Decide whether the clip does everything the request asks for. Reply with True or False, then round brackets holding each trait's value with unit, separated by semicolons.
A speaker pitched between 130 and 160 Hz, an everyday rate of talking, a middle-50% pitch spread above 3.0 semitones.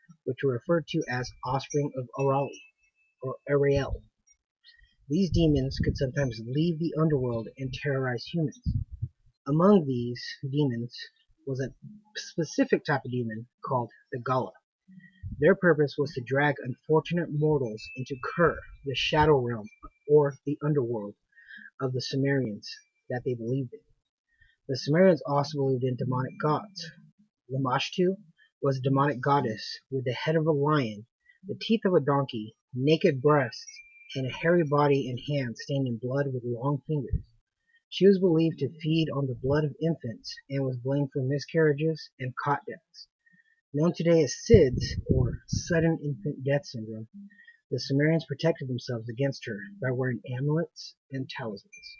True (140 Hz; 150 wpm; 4.1 semitones)